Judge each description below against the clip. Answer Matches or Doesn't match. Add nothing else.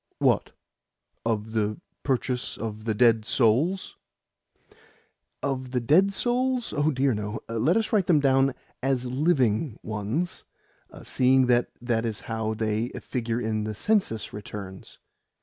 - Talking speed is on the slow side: Matches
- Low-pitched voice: Matches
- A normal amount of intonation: Matches